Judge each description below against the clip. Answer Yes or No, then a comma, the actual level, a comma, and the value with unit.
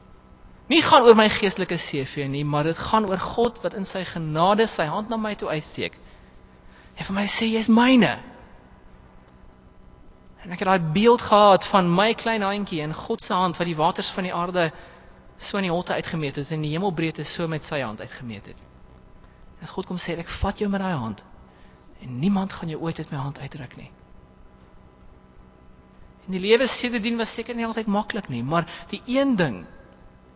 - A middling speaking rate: Yes, average, 195 wpm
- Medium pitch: Yes, medium, 165 Hz